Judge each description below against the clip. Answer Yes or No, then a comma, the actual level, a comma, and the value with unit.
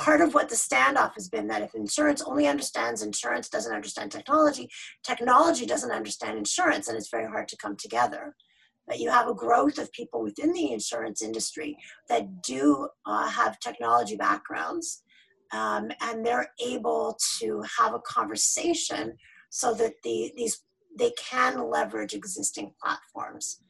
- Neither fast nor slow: Yes, average, 155 wpm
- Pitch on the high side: Yes, very high, 290 Hz